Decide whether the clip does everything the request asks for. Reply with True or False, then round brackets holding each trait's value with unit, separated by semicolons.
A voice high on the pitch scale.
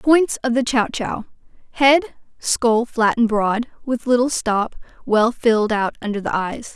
True (235 Hz)